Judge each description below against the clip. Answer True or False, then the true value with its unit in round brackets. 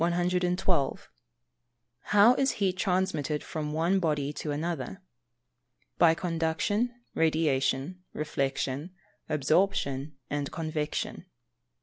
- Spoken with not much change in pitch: False (3.7 semitones)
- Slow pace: True (85 wpm)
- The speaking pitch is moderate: True (165 Hz)